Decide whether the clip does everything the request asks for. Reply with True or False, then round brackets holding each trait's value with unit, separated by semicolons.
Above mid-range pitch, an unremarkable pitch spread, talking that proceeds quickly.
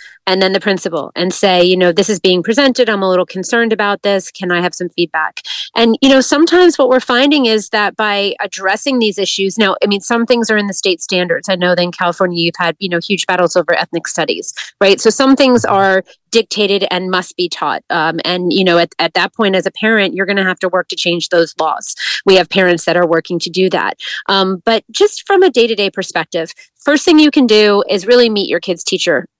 True (195 Hz; 4.0 semitones; 245 wpm)